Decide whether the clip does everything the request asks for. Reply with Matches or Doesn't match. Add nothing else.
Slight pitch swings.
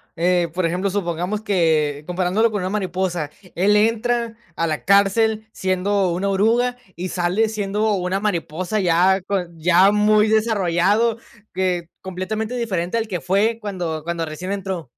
Doesn't match